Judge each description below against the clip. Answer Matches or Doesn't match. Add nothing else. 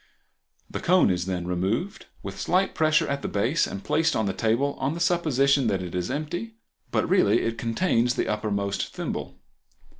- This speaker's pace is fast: Doesn't match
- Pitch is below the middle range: Matches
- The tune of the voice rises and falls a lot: Matches